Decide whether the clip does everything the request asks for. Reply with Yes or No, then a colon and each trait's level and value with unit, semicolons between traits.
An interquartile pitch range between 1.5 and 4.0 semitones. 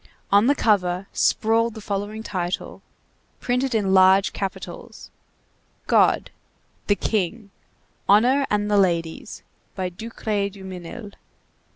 Yes: average, 2.9 semitones